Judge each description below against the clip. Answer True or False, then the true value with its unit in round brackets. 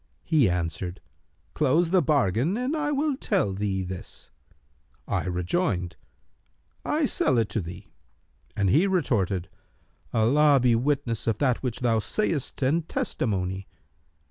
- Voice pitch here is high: False (120 Hz)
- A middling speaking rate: False (130 wpm)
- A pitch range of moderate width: False (8.6 semitones)